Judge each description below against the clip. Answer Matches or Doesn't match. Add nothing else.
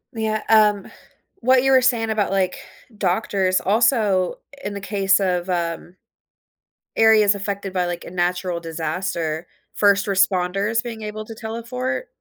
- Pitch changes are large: Doesn't match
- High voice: Matches